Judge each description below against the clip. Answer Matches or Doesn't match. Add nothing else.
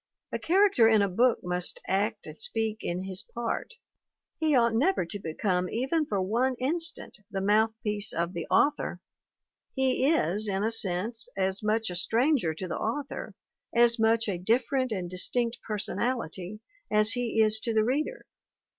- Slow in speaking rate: Doesn't match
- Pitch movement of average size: Matches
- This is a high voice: Matches